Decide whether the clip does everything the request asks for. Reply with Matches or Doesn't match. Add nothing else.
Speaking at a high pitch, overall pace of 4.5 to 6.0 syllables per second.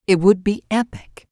Matches